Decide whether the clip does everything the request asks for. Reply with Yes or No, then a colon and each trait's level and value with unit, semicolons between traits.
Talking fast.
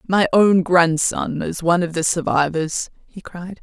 No: average, 165 wpm